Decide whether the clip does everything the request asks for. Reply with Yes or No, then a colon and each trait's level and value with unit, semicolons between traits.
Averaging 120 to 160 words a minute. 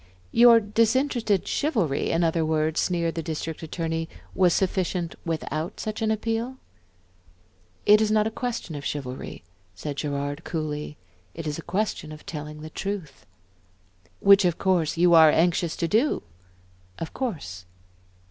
Yes: average, 145 wpm